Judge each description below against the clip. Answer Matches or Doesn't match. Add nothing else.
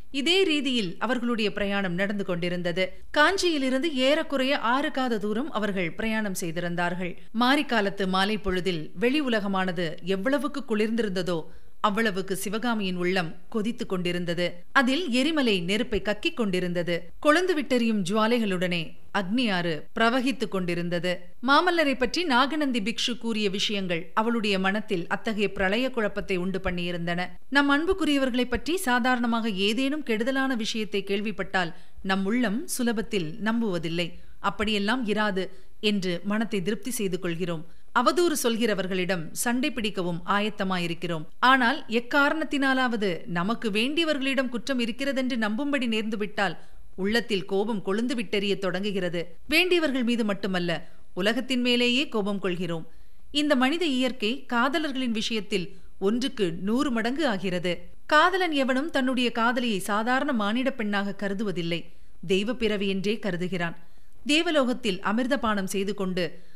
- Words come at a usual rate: Matches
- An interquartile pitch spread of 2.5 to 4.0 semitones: Doesn't match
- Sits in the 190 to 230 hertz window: Matches